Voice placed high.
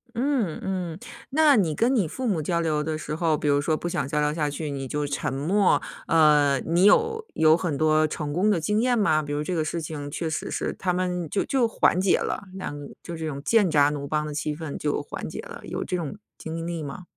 No: medium, 160 Hz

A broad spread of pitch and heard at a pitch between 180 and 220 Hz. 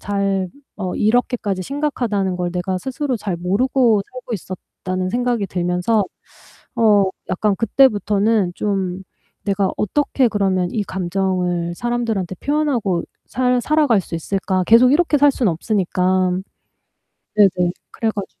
No: average, 4.6 semitones; high, 200 Hz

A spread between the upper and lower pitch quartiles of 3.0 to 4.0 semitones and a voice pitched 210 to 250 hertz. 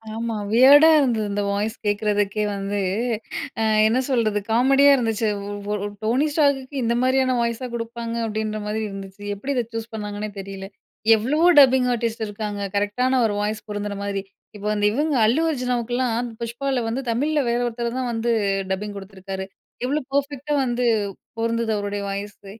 Yes: average, 3.6 semitones; high, 230 Hz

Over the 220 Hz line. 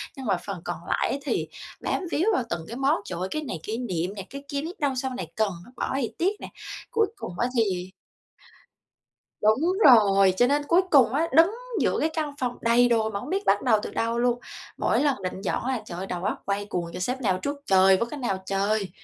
Yes: high, 235 Hz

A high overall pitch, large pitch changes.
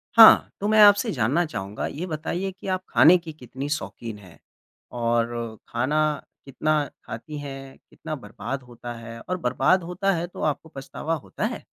No: medium, 145 Hz; wide, 6.3 semitones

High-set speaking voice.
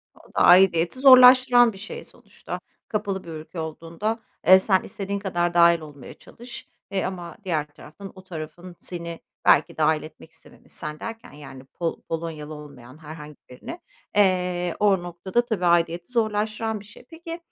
No: medium, 175 Hz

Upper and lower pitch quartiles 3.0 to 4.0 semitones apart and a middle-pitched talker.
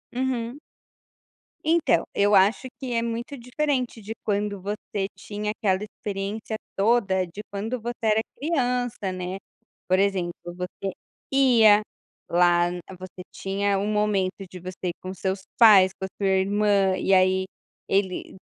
No: average, 3.4 semitones; high, 200 Hz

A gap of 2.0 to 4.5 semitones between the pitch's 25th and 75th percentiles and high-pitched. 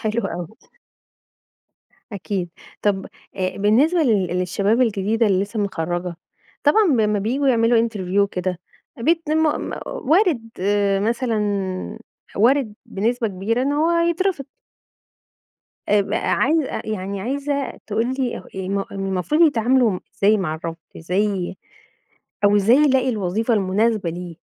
No: average, 5.0 semitones; high, 215 Hz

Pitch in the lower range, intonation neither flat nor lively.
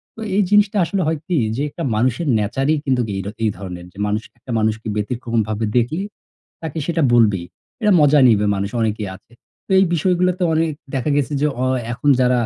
No: low, 125 Hz; wide, 7.0 semitones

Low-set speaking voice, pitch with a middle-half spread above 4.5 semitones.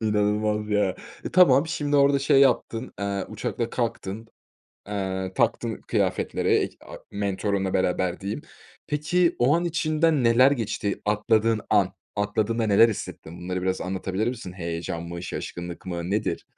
Yes: low, 105 Hz; average, 4.9 semitones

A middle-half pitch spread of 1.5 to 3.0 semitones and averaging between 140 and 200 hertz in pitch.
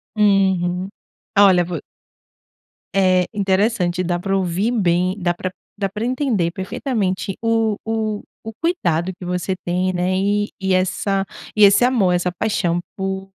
Yes: narrow, 2.5 semitones; high, 190 Hz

